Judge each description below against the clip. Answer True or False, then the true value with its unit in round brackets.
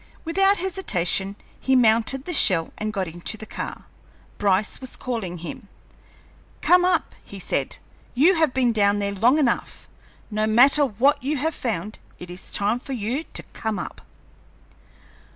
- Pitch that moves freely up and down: True (5.9 semitones)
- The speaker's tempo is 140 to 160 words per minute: True (155 wpm)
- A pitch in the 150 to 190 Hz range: False (235 Hz)